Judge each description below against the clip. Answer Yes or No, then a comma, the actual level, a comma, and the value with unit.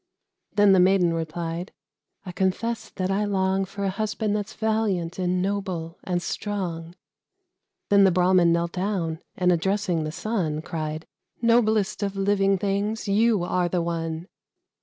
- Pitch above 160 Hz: Yes, high, 190 Hz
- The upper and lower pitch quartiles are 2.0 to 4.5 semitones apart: Yes, average, 3.0 semitones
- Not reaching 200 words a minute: Yes, average, 145 wpm